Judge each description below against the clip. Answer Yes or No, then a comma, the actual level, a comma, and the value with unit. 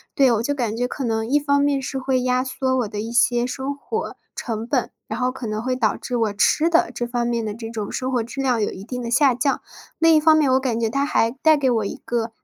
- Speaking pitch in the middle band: No, very high, 250 Hz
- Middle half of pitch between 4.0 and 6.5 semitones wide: No, average, 3.1 semitones